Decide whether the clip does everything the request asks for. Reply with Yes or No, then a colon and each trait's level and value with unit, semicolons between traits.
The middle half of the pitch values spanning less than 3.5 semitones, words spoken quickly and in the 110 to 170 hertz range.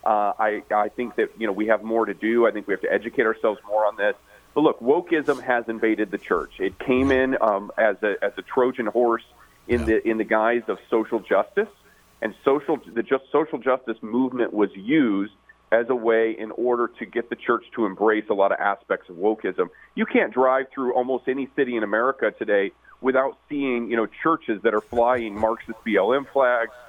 Yes: average, 2.9 semitones; fast, 210 wpm; low, 120 Hz